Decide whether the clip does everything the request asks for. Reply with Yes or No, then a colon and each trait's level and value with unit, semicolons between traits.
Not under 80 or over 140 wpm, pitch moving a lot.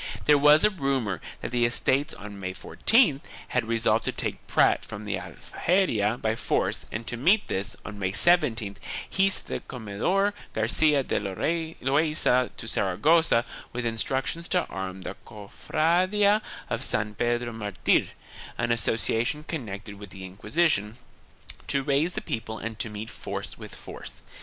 No: average, 160 wpm; wide, 6.8 semitones